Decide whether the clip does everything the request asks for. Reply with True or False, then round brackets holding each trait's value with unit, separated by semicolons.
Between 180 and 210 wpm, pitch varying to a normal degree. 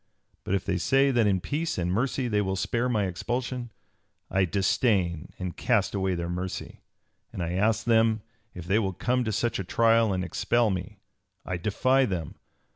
True (185 wpm; 4.3 semitones)